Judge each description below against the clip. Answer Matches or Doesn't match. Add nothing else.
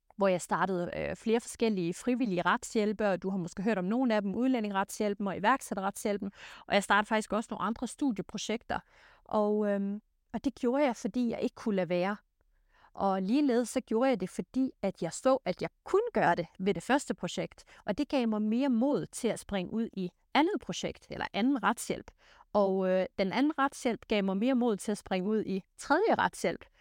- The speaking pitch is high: Matches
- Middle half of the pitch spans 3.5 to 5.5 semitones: Matches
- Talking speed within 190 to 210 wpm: Matches